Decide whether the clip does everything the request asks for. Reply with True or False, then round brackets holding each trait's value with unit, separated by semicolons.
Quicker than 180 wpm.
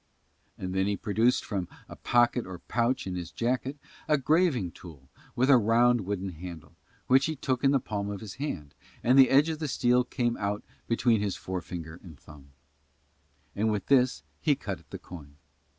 True (190 wpm)